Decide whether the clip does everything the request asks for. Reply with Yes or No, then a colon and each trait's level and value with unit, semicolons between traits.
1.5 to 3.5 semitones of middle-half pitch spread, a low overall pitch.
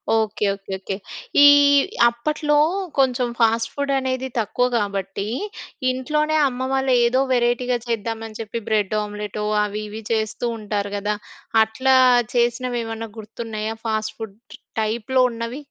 No: average, 3.0 semitones; high, 225 Hz